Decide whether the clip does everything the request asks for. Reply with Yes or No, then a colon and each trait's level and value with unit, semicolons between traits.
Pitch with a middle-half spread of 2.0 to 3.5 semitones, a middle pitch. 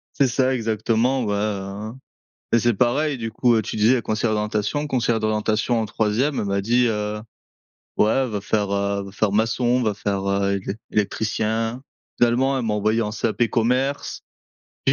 No: narrow, 2.5 semitones; low, 110 Hz